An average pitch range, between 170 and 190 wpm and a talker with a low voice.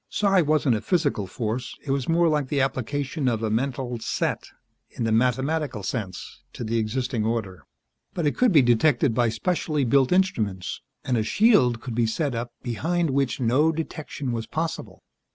Yes: average, 5.0 semitones; average, 175 wpm; low, 130 Hz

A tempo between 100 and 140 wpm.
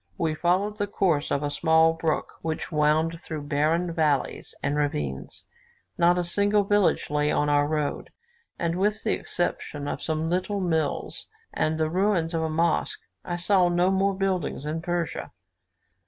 No: average, 165 wpm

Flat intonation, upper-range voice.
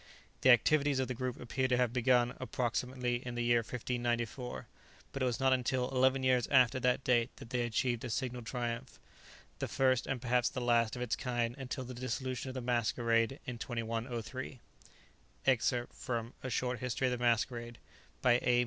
No: narrow, 1.4 semitones; low, 125 Hz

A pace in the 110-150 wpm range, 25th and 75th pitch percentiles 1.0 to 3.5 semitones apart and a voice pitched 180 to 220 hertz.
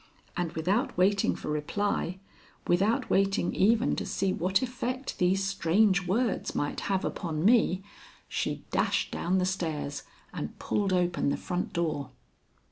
Yes: average, 140 wpm; average, 3.0 semitones; high, 190 Hz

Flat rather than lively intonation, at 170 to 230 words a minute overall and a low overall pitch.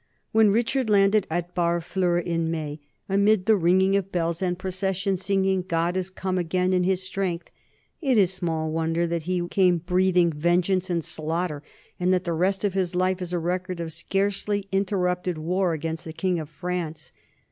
No: narrow, 2.1 semitones; average, 180 wpm; medium, 180 Hz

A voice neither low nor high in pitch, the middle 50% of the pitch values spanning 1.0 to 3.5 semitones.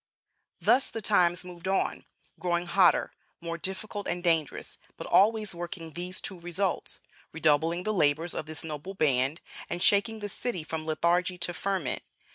Yes: medium, 175 Hz; average, 2.8 semitones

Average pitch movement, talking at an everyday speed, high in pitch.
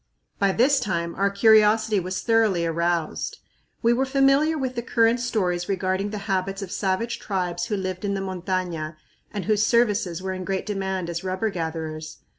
Yes: average, 3.5 semitones; average, 175 wpm; high, 195 Hz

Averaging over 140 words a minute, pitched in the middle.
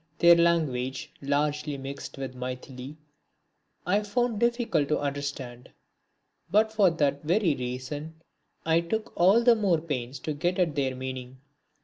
No: slow, 135 wpm; medium, 150 Hz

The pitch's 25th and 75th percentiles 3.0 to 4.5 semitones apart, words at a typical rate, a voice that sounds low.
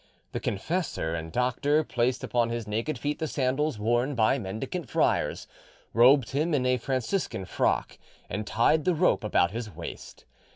No: average, 5.0 semitones; average, 160 wpm; low, 125 Hz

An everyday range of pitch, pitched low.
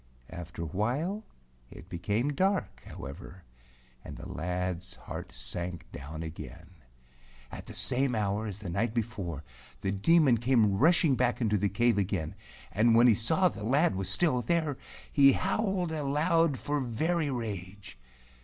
No: wide, 7.3 semitones; low, 115 Hz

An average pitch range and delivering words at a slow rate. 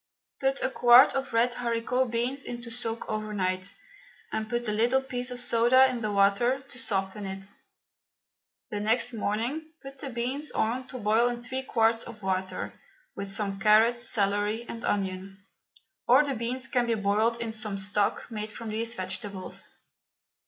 No: average, 3.0 semitones; average, 165 wpm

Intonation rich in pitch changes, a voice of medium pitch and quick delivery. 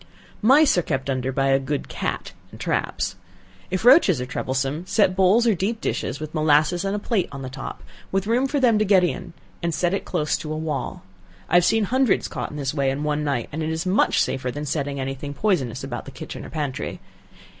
Yes: wide, 6.1 semitones; medium, 155 Hz; fast, 230 wpm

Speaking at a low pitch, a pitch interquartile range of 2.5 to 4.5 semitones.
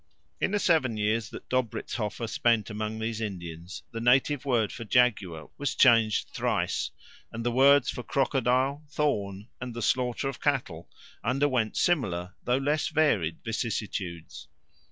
Yes: low, 115 Hz; average, 4.2 semitones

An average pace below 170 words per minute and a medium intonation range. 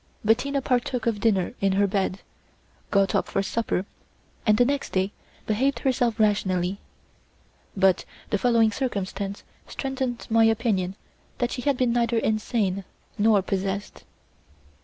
Yes: slow, 135 wpm; average, 3.7 semitones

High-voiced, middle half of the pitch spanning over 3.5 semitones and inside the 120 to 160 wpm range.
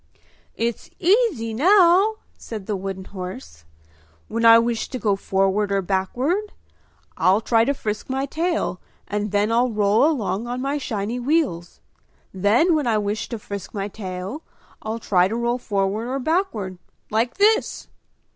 Yes: high, 225 Hz; wide, 5.5 semitones; average, 155 wpm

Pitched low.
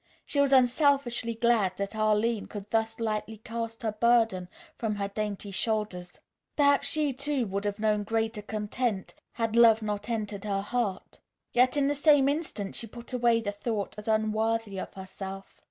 No: high, 220 Hz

